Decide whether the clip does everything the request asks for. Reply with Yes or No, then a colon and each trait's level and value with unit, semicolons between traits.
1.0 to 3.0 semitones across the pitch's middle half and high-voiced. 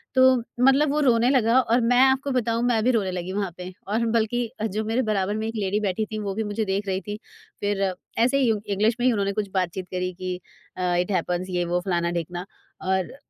No: average, 3.9 semitones; high, 205 Hz